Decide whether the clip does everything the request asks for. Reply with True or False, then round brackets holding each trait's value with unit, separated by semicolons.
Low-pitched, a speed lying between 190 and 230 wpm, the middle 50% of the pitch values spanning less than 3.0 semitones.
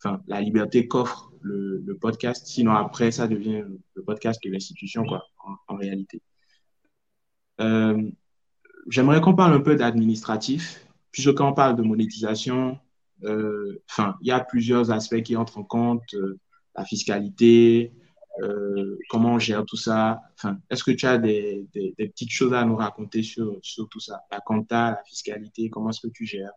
False (110 Hz; 175 wpm; 2.4 semitones)